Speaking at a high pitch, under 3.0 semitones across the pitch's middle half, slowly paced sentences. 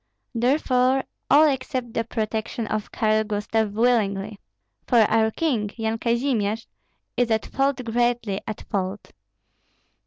Yes: high, 225 Hz; narrow, 2.6 semitones; slow, 120 wpm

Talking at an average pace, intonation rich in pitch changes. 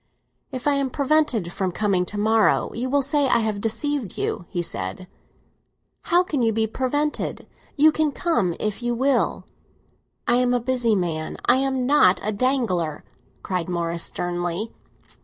Yes: average, 155 wpm; wide, 6.8 semitones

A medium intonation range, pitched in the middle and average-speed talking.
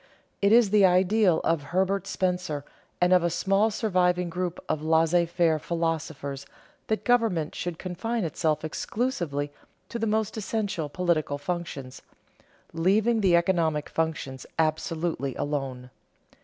No: average, 3.8 semitones; medium, 175 Hz; slow, 130 wpm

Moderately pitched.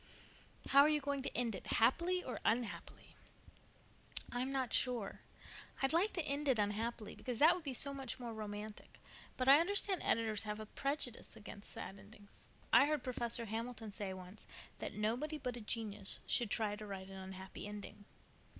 No: high, 235 Hz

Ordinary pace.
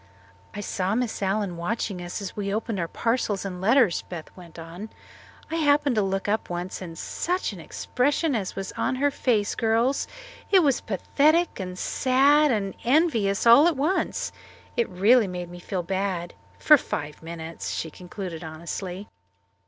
Yes: average, 165 wpm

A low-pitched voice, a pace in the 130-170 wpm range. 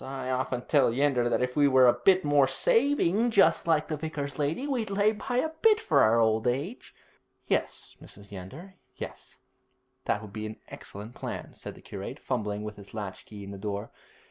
No: low, 130 Hz; average, 195 wpm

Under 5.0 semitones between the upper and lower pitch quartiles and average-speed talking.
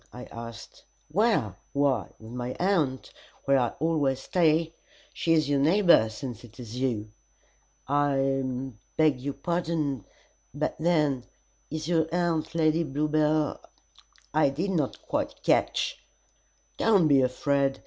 No: average, 3.8 semitones; slow, 130 wpm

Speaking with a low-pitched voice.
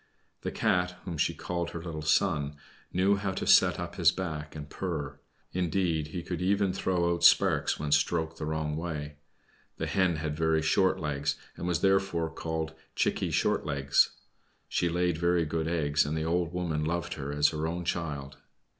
Yes: very low, 80 Hz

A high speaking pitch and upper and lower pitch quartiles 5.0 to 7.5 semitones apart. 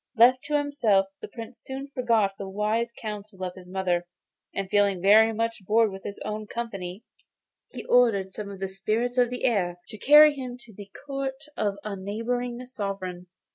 No: high, 215 Hz; average, 3.9 semitones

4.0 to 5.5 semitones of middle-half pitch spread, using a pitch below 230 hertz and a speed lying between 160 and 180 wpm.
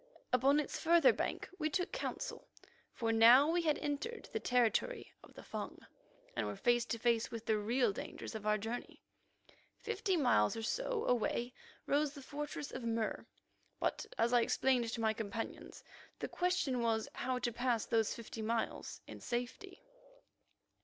No: average, 4.5 semitones; high, 245 Hz; average, 165 wpm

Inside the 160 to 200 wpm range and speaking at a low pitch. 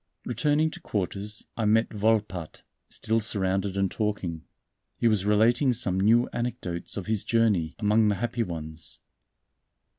No: average, 140 wpm; low, 105 Hz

